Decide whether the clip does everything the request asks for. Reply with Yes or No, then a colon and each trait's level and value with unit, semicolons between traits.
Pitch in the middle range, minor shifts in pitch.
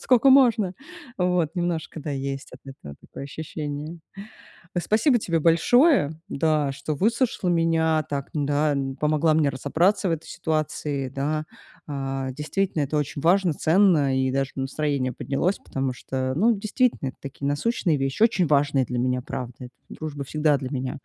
No: medium, 150 Hz; average, 4.2 semitones